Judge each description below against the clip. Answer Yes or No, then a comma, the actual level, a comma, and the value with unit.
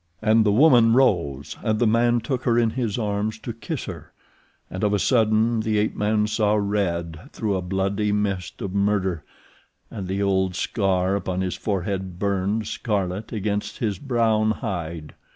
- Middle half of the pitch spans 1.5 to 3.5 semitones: Yes, average, 2.7 semitones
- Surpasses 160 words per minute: Yes, average, 170 wpm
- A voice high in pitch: No, low, 105 Hz